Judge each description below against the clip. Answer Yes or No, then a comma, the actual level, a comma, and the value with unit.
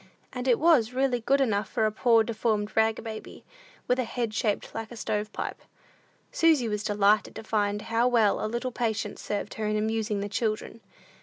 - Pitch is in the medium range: No, high, 220 Hz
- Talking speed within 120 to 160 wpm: No, average, 190 wpm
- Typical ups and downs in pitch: No, narrow, 2.3 semitones